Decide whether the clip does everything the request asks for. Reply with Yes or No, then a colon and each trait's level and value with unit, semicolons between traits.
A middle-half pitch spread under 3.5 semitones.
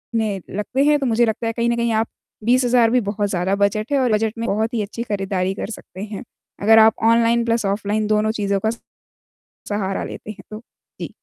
Yes: narrow, 2.6 semitones